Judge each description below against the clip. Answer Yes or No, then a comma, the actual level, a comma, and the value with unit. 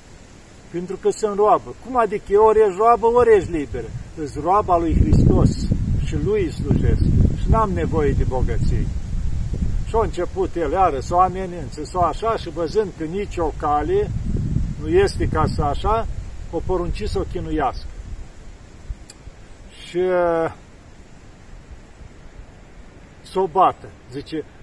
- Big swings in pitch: Yes, wide, 6.8 semitones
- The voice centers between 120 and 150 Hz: No, medium, 180 Hz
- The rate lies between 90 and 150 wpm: Yes, average, 135 wpm